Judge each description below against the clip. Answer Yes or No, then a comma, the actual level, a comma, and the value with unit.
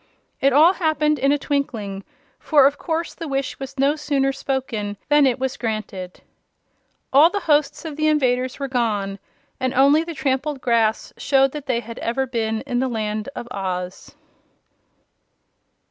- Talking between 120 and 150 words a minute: No, average, 160 wpm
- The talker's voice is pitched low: No, very high, 270 Hz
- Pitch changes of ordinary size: Yes, average, 4.0 semitones